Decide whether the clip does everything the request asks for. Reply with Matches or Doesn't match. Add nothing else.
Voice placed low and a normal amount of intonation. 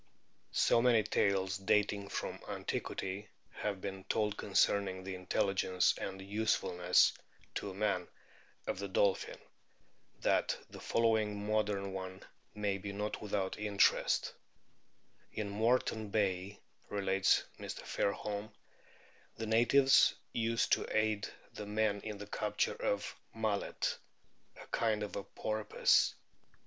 Doesn't match